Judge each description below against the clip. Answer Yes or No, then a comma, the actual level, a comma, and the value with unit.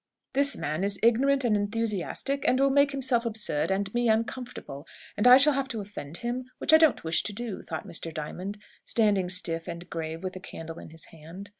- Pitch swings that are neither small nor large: No, wide, 6.7 semitones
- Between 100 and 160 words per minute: No, fast, 205 wpm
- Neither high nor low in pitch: No, high, 205 Hz